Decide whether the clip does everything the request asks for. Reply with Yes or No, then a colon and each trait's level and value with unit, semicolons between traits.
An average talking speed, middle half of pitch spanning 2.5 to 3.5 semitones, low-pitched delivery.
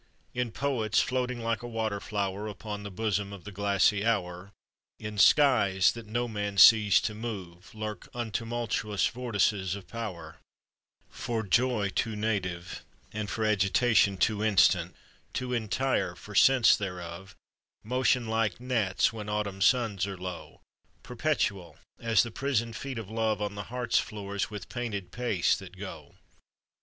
Yes: average, 145 wpm; average, 2.9 semitones; low, 105 Hz